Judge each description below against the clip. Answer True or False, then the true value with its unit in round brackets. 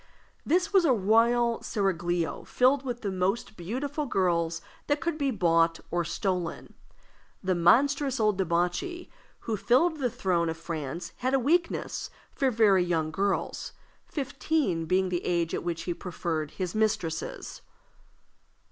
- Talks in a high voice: True (195 Hz)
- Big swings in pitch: True (7.1 semitones)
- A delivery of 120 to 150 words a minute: True (140 wpm)